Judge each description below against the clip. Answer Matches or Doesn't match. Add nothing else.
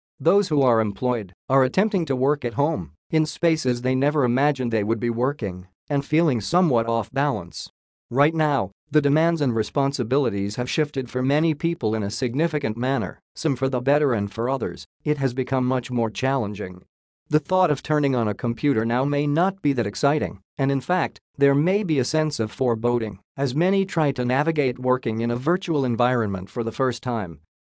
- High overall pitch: Doesn't match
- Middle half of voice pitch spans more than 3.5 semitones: Matches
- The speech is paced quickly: Doesn't match